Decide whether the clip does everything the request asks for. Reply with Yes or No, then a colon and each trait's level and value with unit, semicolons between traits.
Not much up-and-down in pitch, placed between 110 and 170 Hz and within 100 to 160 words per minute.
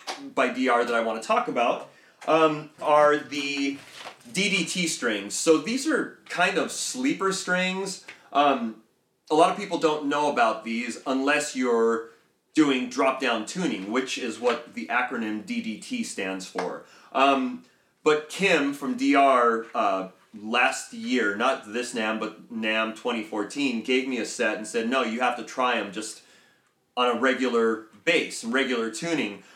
No: wide, 5.6 semitones; low, 135 Hz; average, 155 wpm